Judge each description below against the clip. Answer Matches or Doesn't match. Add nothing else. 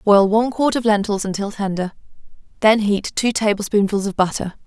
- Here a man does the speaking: Doesn't match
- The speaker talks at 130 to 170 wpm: Matches